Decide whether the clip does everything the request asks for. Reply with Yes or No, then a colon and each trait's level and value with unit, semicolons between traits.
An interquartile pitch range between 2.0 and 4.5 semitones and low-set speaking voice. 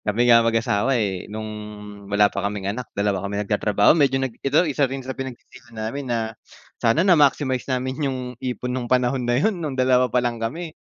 Yes: average, 3.2 semitones; low, 125 Hz